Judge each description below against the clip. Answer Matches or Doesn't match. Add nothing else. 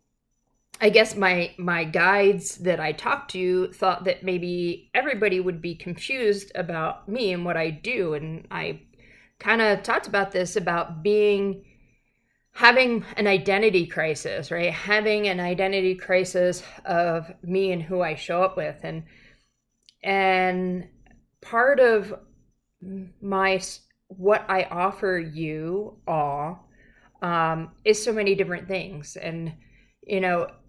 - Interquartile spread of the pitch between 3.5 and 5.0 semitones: Doesn't match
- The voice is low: Doesn't match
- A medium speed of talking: Doesn't match